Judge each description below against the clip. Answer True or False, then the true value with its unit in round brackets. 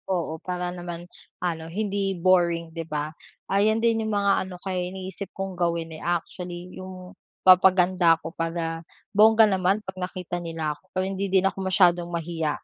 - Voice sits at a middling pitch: True (180 Hz)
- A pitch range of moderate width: False (2.1 semitones)